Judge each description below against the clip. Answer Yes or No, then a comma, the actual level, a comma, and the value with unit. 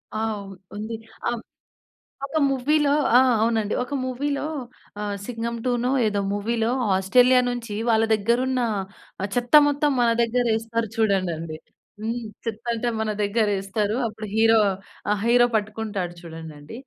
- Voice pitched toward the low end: No, high, 225 Hz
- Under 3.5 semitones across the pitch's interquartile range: Yes, average, 2.9 semitones